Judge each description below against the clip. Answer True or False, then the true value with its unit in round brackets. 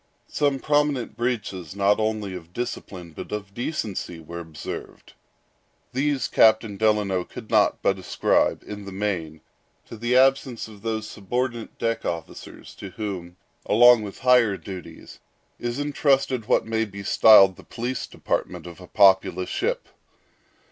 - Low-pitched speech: True (110 Hz)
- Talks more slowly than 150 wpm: True (140 wpm)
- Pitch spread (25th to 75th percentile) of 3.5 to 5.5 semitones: True (4.3 semitones)